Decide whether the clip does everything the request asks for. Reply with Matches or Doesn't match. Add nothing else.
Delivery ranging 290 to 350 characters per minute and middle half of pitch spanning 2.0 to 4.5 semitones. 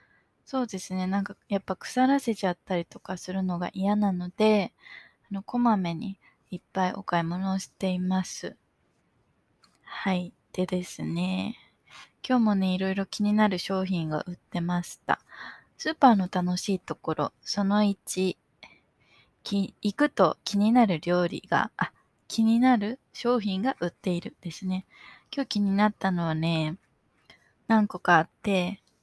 Doesn't match